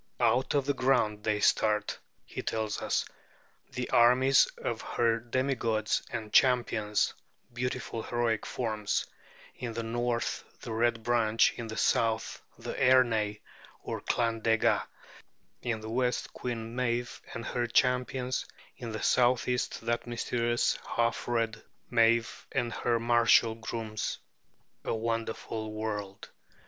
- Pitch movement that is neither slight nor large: No, narrow, 1.5 semitones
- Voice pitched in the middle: No, low, 115 Hz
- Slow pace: Yes, slow, 125 wpm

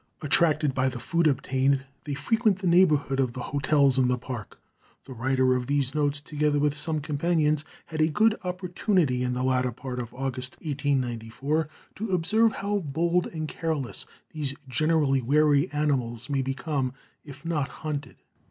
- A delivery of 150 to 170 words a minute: Yes, average, 160 wpm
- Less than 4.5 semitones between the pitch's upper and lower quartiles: Yes, average, 3.3 semitones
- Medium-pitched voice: Yes, medium, 145 Hz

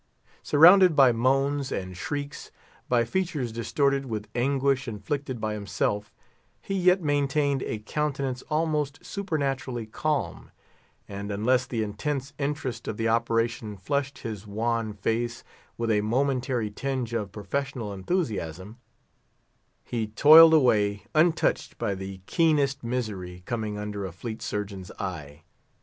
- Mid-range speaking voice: No, low, 120 Hz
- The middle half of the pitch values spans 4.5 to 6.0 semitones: Yes, average, 5.1 semitones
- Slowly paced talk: Yes, slow, 125 wpm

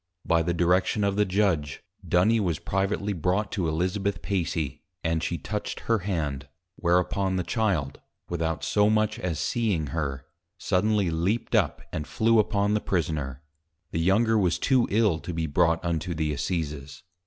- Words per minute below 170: Yes, average, 160 wpm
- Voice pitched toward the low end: Yes, very low, 90 Hz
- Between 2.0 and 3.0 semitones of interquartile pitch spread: No, average, 4.3 semitones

